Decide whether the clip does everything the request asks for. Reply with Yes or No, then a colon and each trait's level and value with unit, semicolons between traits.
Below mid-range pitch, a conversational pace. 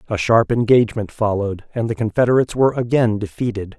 Yes: low, 110 Hz; average, 160 wpm